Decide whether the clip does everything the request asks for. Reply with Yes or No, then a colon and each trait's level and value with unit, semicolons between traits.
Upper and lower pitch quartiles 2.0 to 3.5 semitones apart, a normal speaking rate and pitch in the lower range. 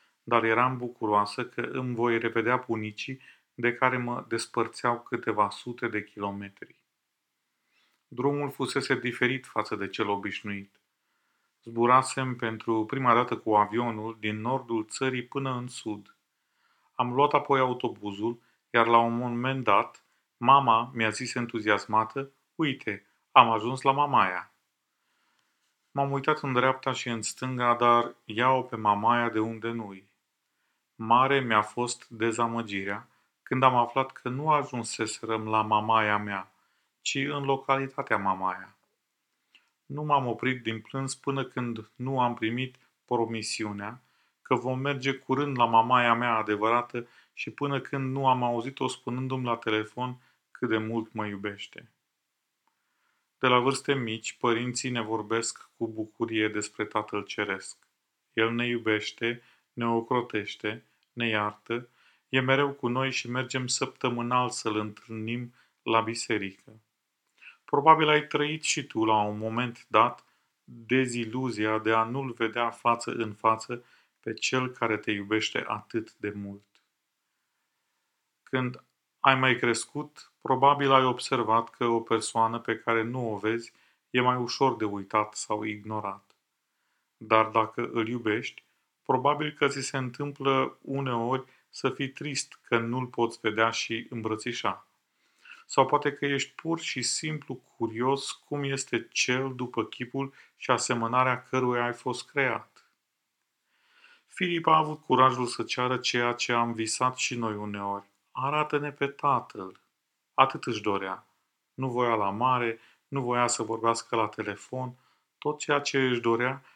Yes: average, 2.8 semitones; average, 135 wpm; low, 120 Hz